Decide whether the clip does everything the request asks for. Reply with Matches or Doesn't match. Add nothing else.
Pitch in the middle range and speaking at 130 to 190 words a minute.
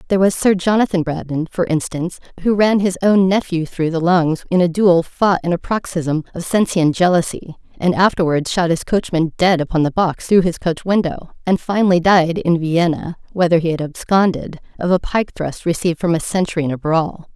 Doesn't match